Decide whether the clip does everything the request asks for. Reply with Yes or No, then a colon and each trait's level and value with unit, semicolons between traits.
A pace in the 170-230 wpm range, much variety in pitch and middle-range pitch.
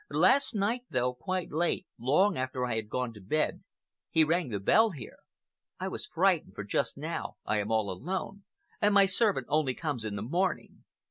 Yes: average, 180 wpm; wide, 8.4 semitones; medium, 150 Hz